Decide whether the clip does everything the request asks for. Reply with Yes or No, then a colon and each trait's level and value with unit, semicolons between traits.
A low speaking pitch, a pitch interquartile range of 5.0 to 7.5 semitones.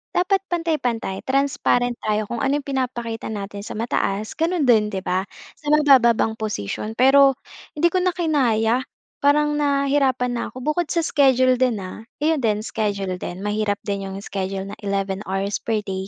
No: high, 235 Hz; wide, 5.6 semitones